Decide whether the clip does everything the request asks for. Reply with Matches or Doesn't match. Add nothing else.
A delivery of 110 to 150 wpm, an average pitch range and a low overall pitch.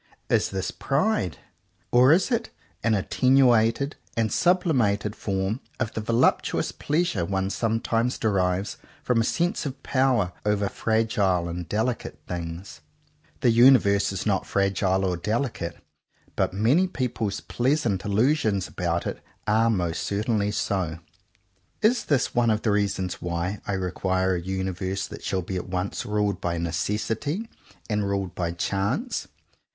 Matches